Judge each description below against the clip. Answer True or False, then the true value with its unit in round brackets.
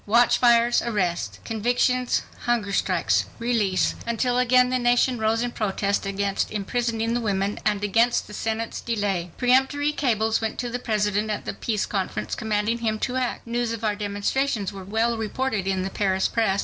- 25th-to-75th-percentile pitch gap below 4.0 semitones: True (3.1 semitones)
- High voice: True (220 Hz)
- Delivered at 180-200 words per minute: False (150 wpm)